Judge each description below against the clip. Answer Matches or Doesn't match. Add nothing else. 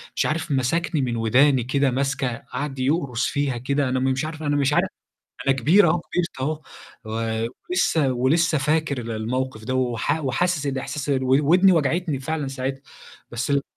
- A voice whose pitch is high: Doesn't match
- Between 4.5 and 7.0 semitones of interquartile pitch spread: Doesn't match